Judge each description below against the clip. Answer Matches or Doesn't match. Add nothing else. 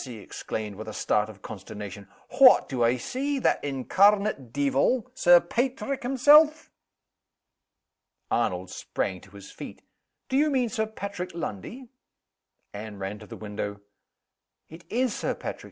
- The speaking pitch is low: Doesn't match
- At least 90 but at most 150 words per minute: Matches